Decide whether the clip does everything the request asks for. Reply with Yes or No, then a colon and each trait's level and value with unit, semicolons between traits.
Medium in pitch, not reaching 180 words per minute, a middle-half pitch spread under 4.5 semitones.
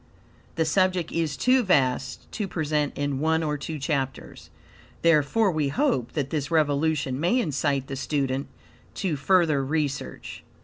Yes: medium, 150 Hz; average, 140 wpm; average, 3.1 semitones